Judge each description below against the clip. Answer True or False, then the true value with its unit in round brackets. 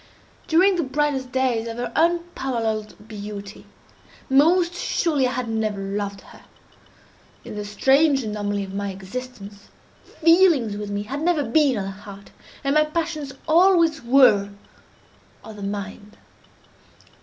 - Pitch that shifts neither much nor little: False (6.8 semitones)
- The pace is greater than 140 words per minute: False (135 wpm)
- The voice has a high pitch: True (245 Hz)